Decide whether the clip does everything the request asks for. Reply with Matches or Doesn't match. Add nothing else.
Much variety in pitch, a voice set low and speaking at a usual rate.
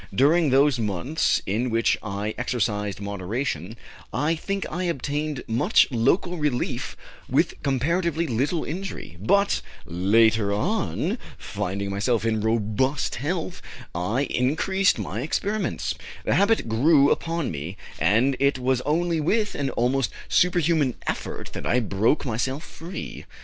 Doesn't match